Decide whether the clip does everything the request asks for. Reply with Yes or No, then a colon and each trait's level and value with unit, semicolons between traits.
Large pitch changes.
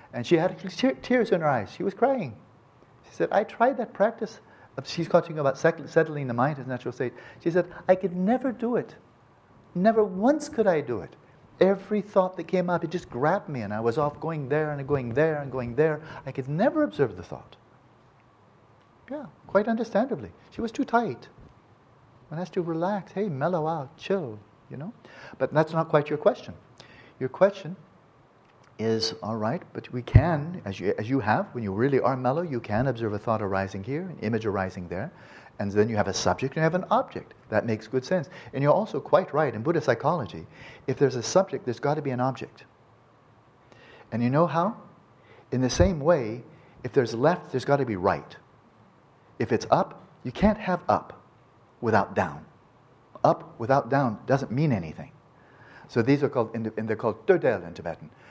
Yes: wide, 7.2 semitones